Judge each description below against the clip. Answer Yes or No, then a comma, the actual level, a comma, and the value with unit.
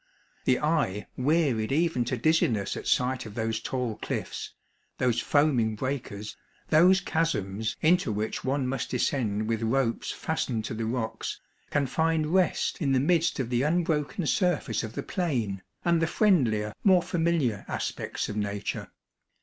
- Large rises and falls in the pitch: Yes, wide, 6.5 semitones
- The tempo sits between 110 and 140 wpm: No, average, 150 wpm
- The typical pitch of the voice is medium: No, low, 130 Hz